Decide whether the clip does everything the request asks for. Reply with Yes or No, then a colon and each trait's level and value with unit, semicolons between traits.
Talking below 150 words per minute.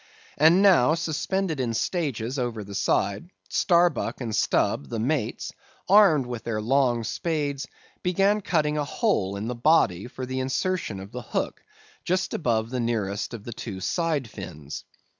No: average, 160 wpm